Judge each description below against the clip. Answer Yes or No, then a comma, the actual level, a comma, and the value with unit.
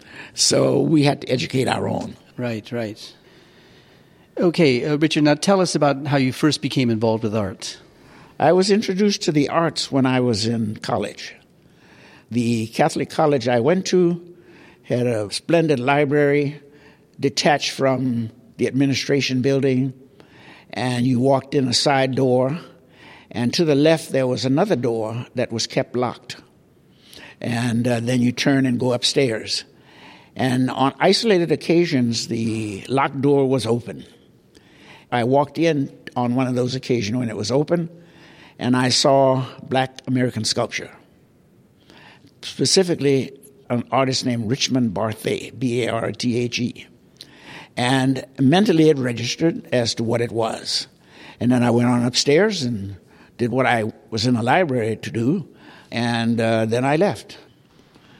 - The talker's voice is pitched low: Yes, low, 130 Hz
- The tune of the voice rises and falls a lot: No, average, 3.4 semitones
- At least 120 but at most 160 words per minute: Yes, average, 150 wpm